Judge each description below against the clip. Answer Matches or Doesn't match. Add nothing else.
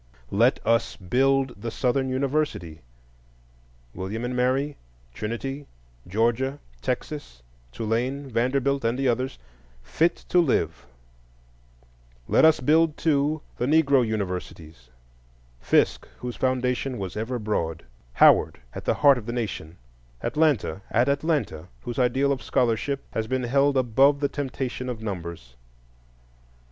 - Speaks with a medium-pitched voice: Doesn't match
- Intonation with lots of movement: Matches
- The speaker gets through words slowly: Matches